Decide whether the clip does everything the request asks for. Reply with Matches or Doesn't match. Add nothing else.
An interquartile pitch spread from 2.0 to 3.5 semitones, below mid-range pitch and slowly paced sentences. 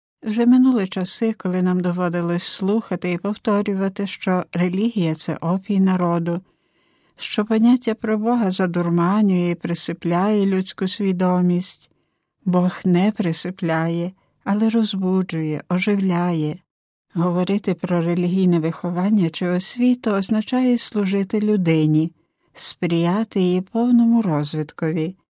Doesn't match